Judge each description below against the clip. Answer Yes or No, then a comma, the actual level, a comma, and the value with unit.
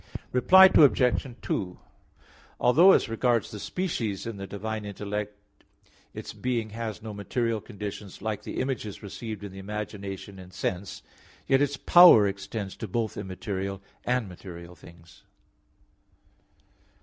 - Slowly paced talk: Yes, slow, 130 wpm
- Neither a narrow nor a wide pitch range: Yes, average, 3.2 semitones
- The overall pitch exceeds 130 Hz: No, low, 105 Hz